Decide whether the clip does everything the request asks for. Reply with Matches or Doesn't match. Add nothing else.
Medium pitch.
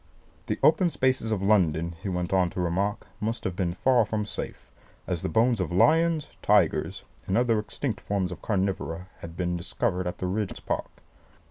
Doesn't match